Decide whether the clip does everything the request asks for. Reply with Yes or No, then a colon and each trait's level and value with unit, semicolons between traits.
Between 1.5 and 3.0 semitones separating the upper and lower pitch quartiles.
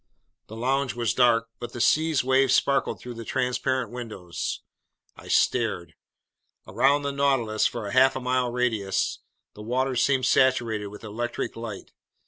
Yes: narrow, 2.5 semitones